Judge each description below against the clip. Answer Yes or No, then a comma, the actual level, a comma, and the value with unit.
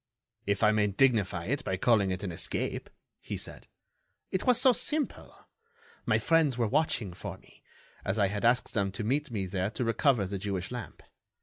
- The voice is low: Yes, low, 110 Hz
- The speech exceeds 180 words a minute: Yes, average, 190 wpm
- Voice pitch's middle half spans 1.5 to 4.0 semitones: No, average, 5.2 semitones